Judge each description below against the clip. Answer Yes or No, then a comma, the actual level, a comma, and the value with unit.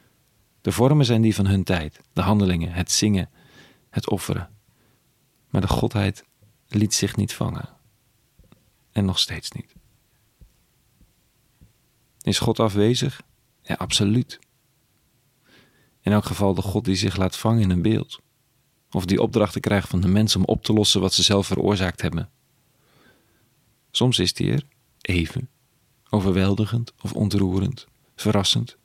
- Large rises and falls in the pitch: No, average, 3.7 semitones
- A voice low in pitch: Yes, low, 105 Hz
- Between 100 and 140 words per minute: Yes, slow, 135 wpm